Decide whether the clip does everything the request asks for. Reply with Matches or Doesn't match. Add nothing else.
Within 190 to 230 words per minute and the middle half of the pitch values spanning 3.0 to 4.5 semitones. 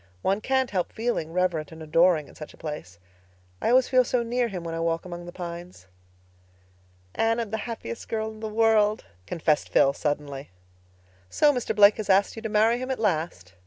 Doesn't match